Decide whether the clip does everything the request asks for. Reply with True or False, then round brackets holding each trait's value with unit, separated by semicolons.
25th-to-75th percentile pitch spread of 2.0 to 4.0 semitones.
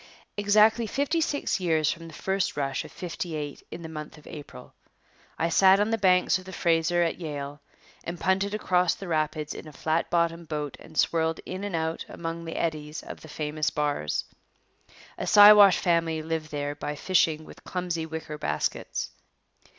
True (3.2 semitones)